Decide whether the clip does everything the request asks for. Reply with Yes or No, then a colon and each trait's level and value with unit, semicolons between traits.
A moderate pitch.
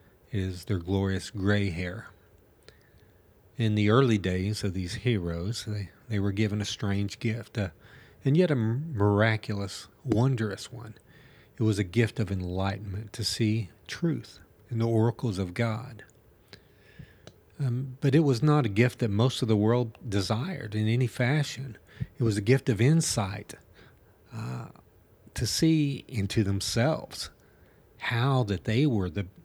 No: low, 110 Hz